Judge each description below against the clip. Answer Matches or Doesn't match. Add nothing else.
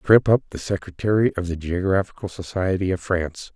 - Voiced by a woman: Doesn't match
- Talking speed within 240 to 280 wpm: Doesn't match